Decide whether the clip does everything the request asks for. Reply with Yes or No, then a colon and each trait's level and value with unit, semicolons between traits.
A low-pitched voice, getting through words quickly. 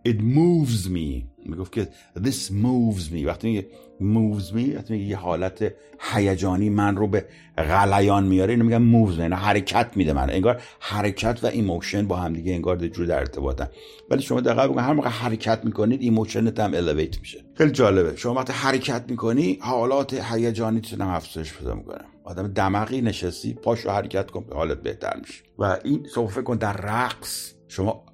Yes: low, 105 Hz; fast, 170 wpm